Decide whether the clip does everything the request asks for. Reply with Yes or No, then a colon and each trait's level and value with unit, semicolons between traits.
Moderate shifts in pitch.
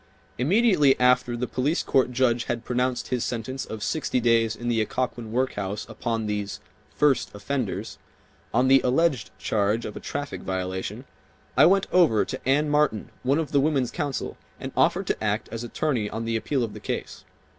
Yes: average, 3.6 semitones